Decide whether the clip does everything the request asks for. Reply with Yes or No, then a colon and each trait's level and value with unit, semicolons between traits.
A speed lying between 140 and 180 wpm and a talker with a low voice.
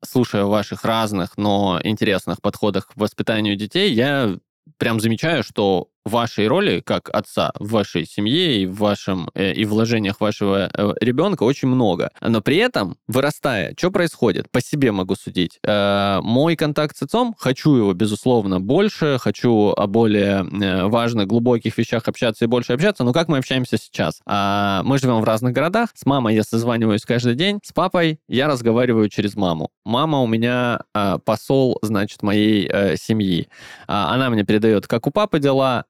Yes: average, 155 wpm; low, 115 Hz